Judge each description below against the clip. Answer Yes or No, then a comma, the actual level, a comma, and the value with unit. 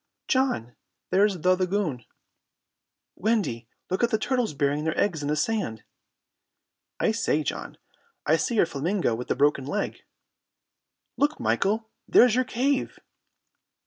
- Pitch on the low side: No, high, 190 Hz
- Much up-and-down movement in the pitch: Yes, wide, 7.5 semitones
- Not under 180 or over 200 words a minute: No, slow, 135 wpm